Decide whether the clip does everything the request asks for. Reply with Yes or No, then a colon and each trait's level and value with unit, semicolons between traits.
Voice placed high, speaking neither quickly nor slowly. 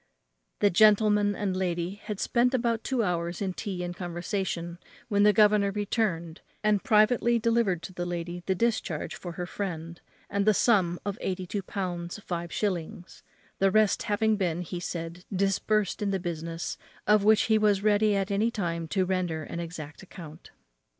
Yes: high, 195 Hz; average, 170 wpm